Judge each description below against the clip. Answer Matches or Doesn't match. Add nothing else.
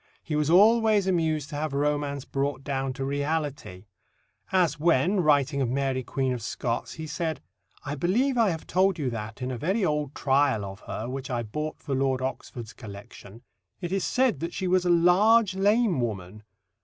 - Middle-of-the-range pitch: Matches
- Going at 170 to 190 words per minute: Matches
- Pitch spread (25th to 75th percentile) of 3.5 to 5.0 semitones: Doesn't match